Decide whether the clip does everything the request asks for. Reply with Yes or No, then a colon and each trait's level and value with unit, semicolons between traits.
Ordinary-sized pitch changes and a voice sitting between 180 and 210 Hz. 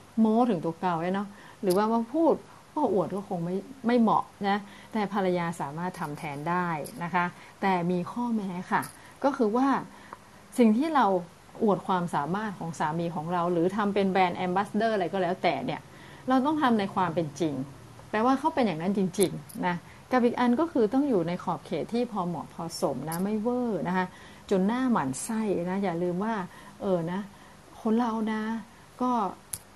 Yes: average, 4.2 semitones; high, 190 Hz